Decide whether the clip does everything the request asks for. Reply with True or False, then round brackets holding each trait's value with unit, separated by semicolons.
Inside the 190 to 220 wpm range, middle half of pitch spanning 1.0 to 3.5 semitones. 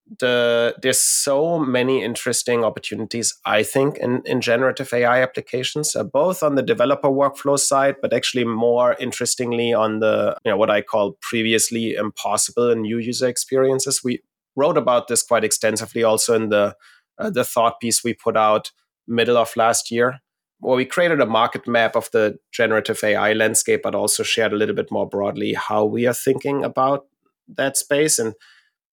False (175 wpm; 2.8 semitones)